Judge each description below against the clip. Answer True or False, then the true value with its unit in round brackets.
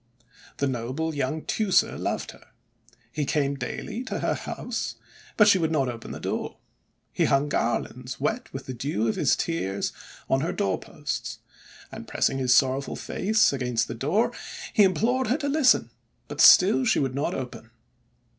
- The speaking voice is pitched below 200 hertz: True (140 Hz)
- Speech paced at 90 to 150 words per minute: False (165 wpm)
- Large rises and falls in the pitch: True (7.8 semitones)